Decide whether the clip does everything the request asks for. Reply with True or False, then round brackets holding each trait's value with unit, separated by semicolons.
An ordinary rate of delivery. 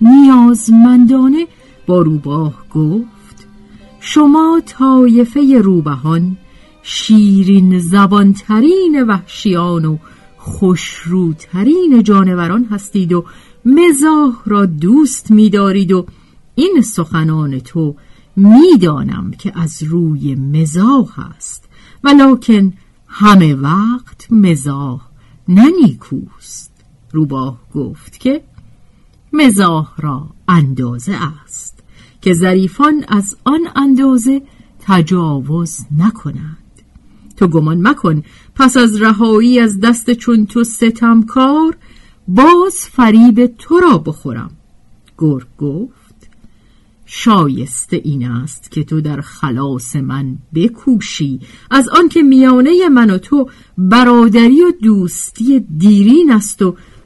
False (95 wpm)